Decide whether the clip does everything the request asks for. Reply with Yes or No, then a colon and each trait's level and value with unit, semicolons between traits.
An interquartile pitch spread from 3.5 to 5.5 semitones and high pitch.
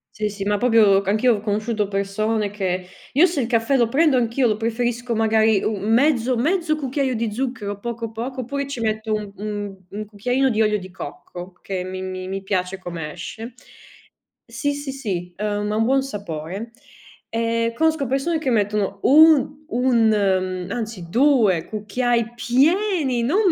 Yes: average, 4.0 semitones; high, 225 Hz